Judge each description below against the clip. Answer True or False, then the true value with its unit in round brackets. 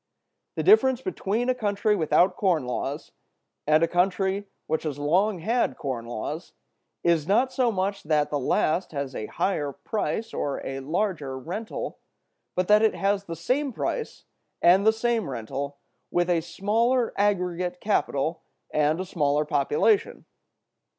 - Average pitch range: False (6.0 semitones)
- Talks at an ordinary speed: True (150 wpm)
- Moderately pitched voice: True (180 Hz)